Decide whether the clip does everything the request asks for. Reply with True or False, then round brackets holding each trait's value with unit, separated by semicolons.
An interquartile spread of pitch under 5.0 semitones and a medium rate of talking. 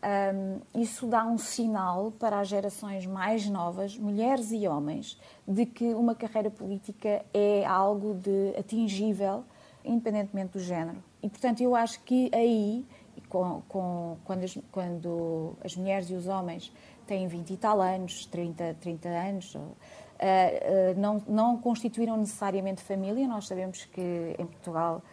True (2.9 semitones; 140 wpm)